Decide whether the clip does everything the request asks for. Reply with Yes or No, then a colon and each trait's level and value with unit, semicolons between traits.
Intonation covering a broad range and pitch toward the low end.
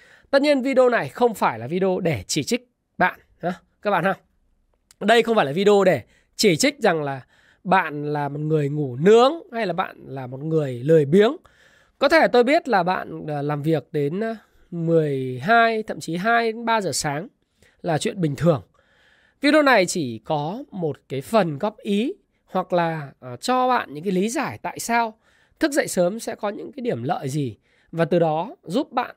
No: wide, 7.1 semitones; high, 190 Hz